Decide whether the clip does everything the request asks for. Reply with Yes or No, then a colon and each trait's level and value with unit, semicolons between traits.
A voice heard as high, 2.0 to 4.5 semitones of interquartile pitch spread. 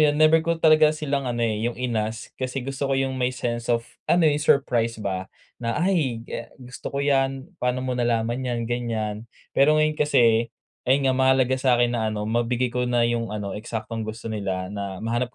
No: low, 120 Hz; average, 2.8 semitones